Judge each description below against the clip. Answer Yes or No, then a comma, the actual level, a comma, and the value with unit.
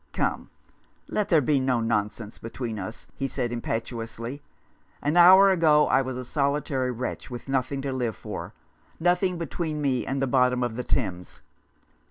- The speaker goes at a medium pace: Yes, average, 175 wpm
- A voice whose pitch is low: Yes, low, 130 Hz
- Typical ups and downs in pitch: Yes, average, 3.9 semitones